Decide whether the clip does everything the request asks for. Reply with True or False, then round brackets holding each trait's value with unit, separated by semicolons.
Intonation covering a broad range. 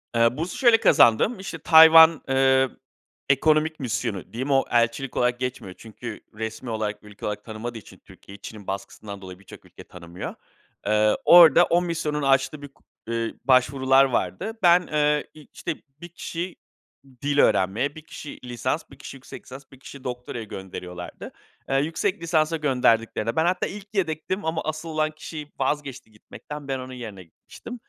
True (5.7 semitones)